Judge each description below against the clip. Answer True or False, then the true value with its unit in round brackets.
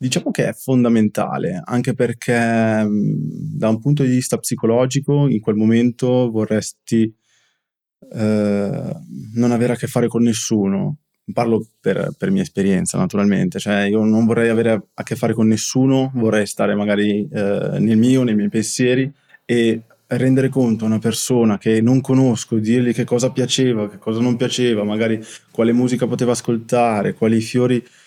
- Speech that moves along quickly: False (155 wpm)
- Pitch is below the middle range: True (115 Hz)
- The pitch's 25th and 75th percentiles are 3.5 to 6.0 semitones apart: False (2.4 semitones)